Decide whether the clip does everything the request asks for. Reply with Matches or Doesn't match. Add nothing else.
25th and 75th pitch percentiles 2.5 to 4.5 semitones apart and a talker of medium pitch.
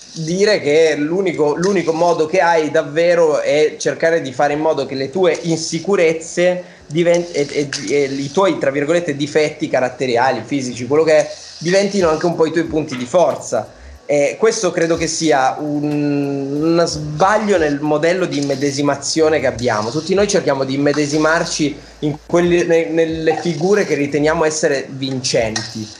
Matches